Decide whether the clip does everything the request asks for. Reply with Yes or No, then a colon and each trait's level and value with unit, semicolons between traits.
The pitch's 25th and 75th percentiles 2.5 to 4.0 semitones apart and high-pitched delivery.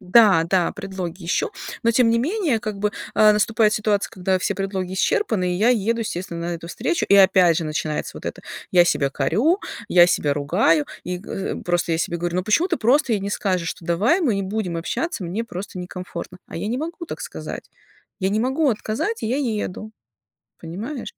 No: average, 4.6 semitones; high, 195 Hz